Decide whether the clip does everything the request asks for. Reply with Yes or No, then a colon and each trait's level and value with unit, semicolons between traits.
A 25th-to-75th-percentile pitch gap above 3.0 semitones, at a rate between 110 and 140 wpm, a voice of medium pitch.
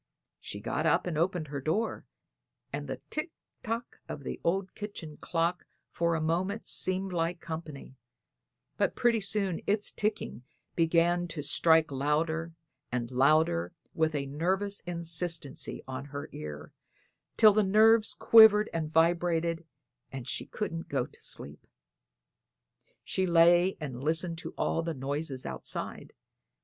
Yes: average, 3.9 semitones; slow, 135 wpm; medium, 165 Hz